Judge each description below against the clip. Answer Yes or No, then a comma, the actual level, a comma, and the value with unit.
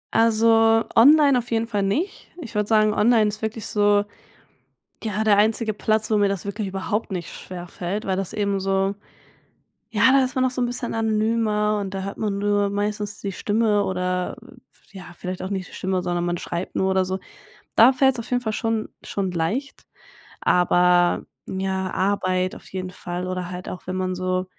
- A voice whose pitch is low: No, high, 205 Hz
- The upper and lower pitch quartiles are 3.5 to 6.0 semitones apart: No, average, 3.1 semitones